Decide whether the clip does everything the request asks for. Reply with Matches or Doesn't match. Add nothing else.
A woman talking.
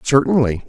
Doesn't match